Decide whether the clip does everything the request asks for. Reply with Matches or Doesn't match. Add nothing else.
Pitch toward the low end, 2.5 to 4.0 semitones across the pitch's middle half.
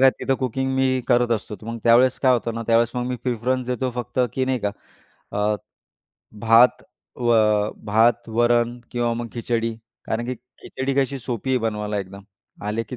Doesn't match